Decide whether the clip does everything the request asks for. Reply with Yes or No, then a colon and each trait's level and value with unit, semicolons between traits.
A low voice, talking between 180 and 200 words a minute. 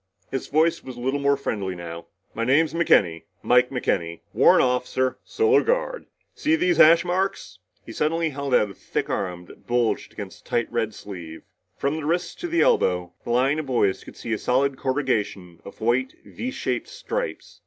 Yes: low, 130 Hz; average, 185 wpm